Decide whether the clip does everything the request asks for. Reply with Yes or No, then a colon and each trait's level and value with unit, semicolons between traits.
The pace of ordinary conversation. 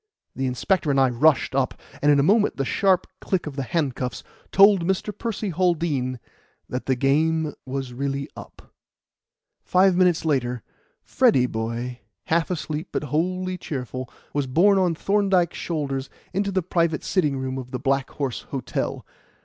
Yes: average, 155 wpm